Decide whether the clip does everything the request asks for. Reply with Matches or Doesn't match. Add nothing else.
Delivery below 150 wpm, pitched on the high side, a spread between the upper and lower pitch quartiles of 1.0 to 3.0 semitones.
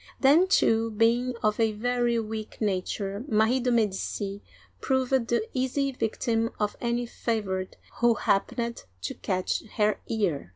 Matches